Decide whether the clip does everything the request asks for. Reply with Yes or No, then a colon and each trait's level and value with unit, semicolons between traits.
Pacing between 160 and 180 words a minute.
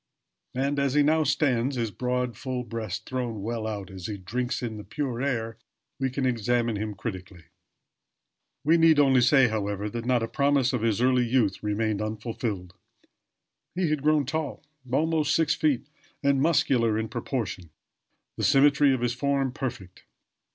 Yes: average, 165 wpm